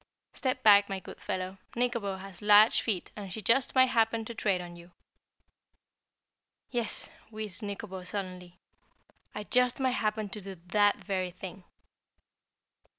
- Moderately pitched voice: No, high, 205 Hz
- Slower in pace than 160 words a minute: Yes, average, 145 wpm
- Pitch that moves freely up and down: No, average, 3.2 semitones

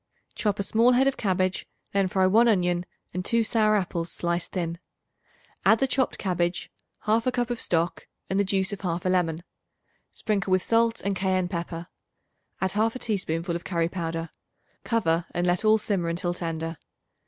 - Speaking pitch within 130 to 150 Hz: No, medium, 185 Hz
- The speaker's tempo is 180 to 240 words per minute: No, average, 170 wpm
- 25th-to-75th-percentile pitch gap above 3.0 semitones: Yes, average, 3.9 semitones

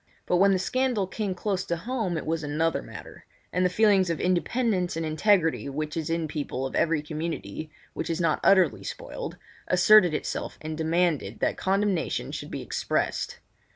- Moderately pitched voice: Yes, medium, 170 Hz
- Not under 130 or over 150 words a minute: No, average, 170 wpm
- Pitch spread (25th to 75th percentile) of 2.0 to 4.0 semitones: Yes, average, 3.6 semitones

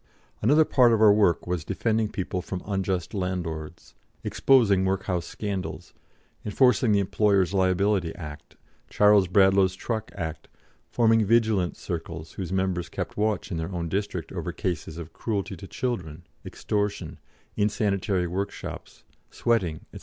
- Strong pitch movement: No, average, 3.1 semitones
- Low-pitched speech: Yes, very low, 95 Hz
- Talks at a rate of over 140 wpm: No, slow, 135 wpm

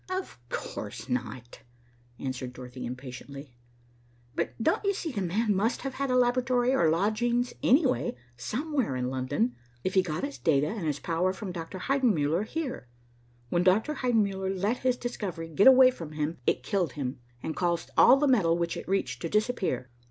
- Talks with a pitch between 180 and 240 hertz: Yes, high, 190 Hz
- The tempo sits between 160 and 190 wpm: Yes, average, 175 wpm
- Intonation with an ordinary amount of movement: No, wide, 9.0 semitones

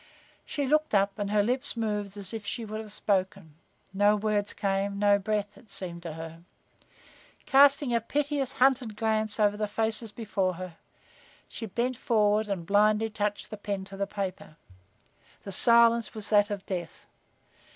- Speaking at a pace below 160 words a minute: No, average, 165 wpm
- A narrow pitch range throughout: Yes, narrow, 2.2 semitones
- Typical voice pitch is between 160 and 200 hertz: No, high, 210 Hz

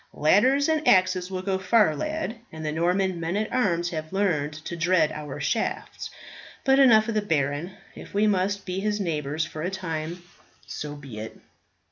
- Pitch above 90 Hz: Yes, medium, 185 Hz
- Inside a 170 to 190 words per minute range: Yes, average, 180 wpm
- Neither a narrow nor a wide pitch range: Yes, average, 4.6 semitones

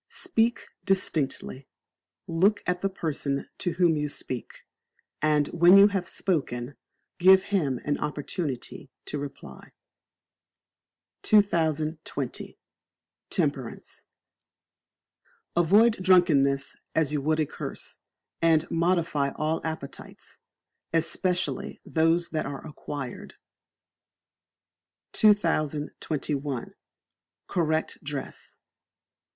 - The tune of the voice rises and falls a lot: No, average, 3.9 semitones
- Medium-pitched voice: Yes, medium, 160 Hz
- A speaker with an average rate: No, slow, 85 wpm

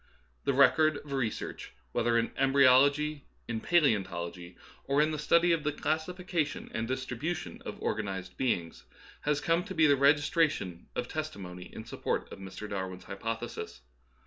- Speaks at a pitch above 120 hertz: Yes, low, 135 Hz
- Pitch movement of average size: No, wide, 6.7 semitones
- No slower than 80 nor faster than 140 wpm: No, average, 160 wpm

